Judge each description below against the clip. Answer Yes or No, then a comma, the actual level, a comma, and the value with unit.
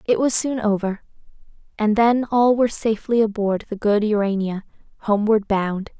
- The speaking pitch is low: No, high, 215 Hz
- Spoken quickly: No, average, 150 wpm